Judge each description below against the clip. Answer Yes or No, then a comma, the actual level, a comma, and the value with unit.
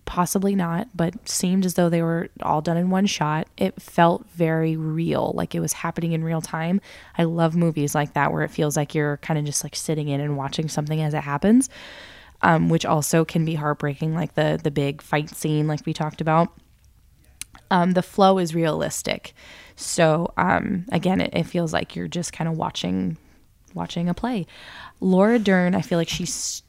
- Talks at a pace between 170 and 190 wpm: No, average, 200 wpm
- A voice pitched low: No, medium, 165 Hz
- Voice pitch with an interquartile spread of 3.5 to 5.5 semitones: No, narrow, 2.6 semitones